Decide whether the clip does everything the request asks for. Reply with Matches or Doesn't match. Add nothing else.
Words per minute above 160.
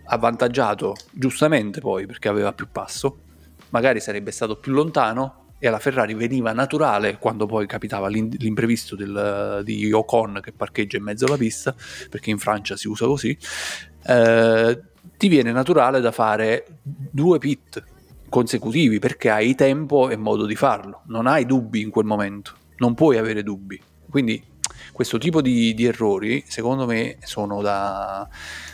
Doesn't match